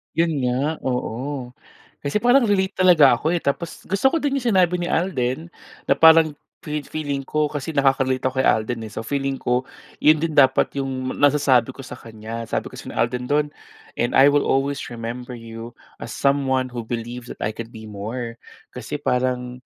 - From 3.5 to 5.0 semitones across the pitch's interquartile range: Yes, average, 3.8 semitones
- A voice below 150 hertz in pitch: Yes, low, 135 Hz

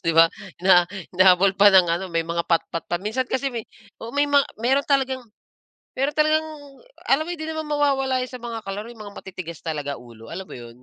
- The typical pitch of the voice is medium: No, high, 210 Hz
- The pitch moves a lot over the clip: Yes, wide, 7.9 semitones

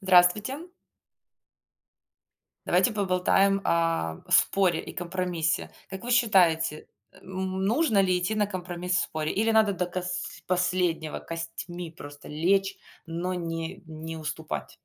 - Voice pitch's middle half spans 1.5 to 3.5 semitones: Yes, average, 2.7 semitones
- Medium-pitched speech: Yes, medium, 180 Hz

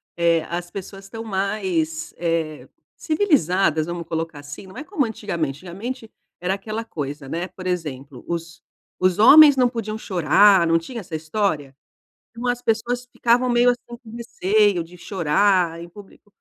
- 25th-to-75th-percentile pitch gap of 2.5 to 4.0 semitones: No, average, 5.2 semitones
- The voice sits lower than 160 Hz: No, medium, 185 Hz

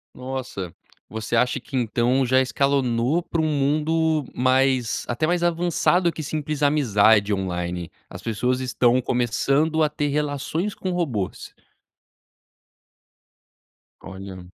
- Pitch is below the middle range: Yes, low, 130 Hz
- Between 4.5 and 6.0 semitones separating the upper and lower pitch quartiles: Yes, average, 4.8 semitones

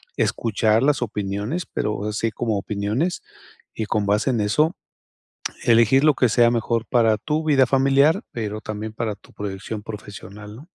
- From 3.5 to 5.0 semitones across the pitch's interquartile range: Yes, average, 4.1 semitones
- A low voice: Yes, low, 110 Hz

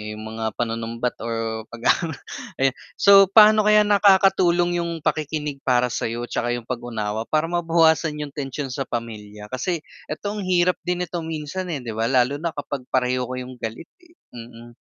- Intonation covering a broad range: Yes, wide, 6.5 semitones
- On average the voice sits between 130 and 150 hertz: Yes, low, 135 Hz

